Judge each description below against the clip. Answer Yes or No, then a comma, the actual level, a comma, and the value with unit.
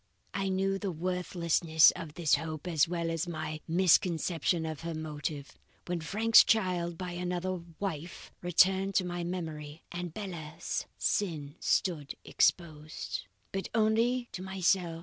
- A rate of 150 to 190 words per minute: No, average, 140 wpm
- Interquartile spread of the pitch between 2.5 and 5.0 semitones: Yes, average, 2.9 semitones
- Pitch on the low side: No, medium, 175 Hz